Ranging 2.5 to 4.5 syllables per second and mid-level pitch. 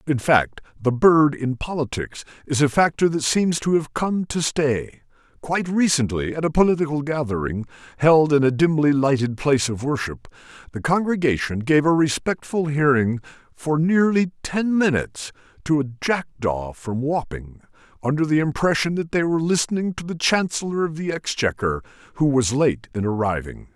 No: 5.0 syllables/s; medium, 145 Hz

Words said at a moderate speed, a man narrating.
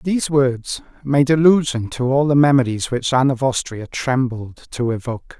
Yes: average, 165 wpm; male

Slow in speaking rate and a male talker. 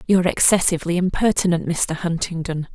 No: slow, 110 wpm; female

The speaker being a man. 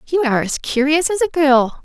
No: female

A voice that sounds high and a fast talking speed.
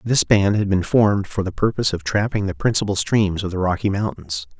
No: low, 100 Hz; fast, 220 wpm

